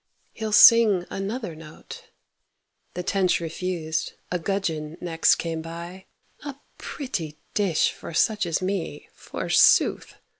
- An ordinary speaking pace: No, slow, 115 wpm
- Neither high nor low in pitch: Yes, medium, 180 Hz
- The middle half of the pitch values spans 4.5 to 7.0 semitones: No, average, 3.6 semitones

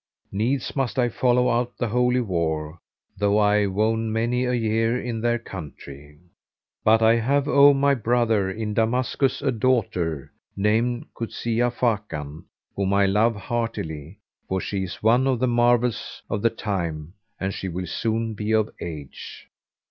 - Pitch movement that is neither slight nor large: Yes, average, 3.9 semitones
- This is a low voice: Yes, low, 110 Hz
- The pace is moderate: Yes, average, 155 wpm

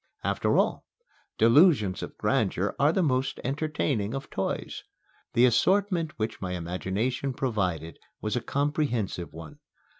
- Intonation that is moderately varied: No, wide, 7.0 semitones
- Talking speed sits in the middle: No, slow, 125 wpm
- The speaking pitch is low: Yes, low, 125 Hz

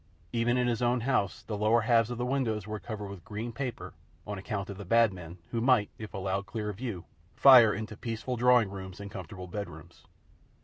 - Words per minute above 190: Yes, fast, 205 wpm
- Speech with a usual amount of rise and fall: Yes, average, 3.2 semitones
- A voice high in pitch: No, low, 110 Hz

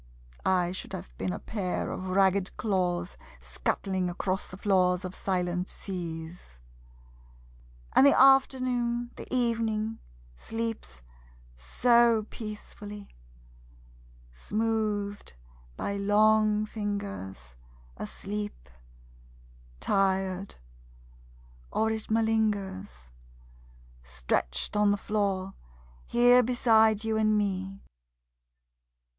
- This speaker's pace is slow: Yes, slow, 85 wpm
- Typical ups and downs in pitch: Yes, average, 3.2 semitones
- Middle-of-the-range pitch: No, high, 205 Hz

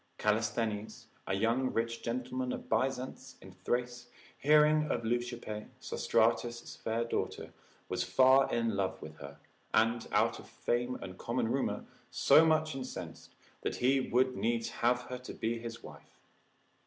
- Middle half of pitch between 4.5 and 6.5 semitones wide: No, narrow, 2.4 semitones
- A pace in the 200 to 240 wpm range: No, average, 145 wpm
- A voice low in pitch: Yes, low, 120 Hz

